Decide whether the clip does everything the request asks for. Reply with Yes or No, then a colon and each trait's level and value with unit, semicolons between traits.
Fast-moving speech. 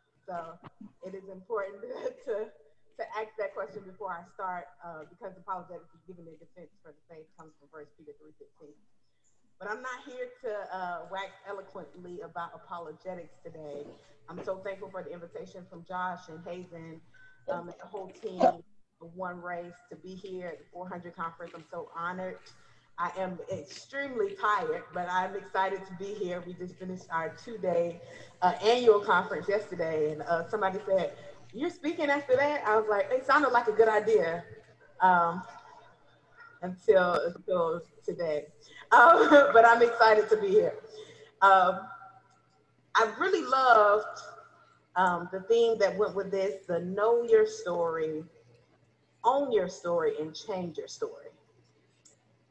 No: average, 155 wpm